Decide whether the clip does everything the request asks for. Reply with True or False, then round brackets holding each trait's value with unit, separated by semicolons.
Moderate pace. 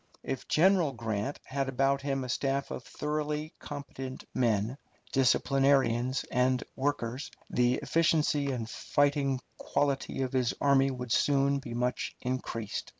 False (130 wpm)